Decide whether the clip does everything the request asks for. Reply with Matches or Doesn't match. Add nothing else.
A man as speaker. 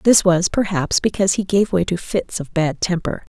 Doesn't match